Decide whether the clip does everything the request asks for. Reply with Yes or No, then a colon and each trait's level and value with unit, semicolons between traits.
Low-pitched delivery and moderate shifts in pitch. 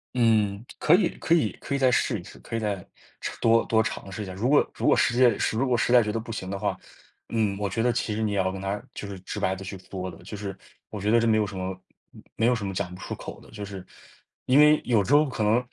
Yes: low, 105 Hz; average, 3.4 semitones